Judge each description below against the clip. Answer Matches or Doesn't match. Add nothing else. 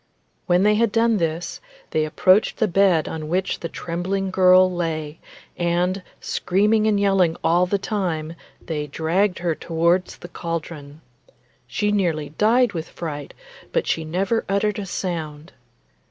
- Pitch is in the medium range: Matches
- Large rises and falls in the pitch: Doesn't match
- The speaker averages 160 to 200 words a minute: Doesn't match